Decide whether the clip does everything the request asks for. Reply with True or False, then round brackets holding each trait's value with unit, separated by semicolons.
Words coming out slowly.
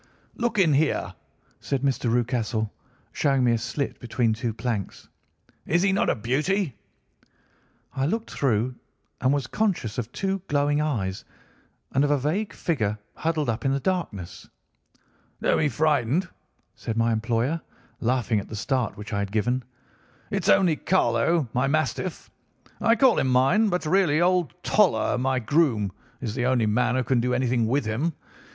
False (160 wpm)